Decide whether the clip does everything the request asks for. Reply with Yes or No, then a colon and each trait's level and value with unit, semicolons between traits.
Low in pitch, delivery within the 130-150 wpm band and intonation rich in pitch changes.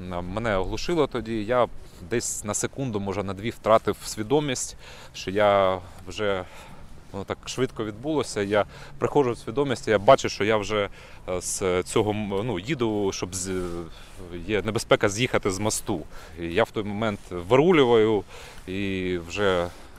No: low, 105 Hz; average, 140 wpm; average, 3.8 semitones